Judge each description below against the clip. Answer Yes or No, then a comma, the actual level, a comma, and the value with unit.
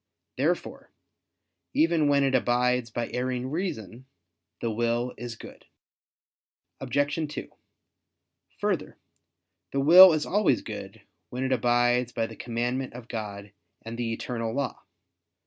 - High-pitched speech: No, low, 125 Hz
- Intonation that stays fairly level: No, average, 3.0 semitones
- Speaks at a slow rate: Yes, slow, 125 wpm